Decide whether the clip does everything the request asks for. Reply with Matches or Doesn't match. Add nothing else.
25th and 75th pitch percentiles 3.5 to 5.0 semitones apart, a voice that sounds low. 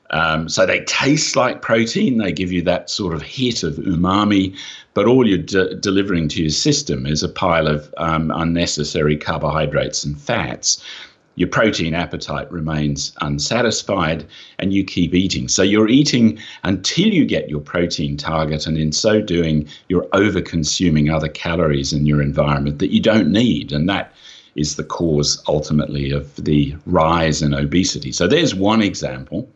Matches